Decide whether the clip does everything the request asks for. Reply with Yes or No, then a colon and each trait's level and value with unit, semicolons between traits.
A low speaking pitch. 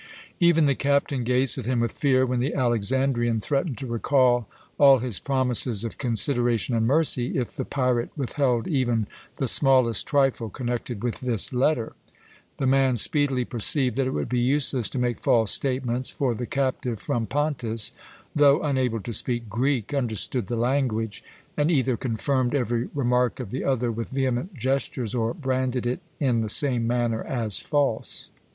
Yes: low, 125 Hz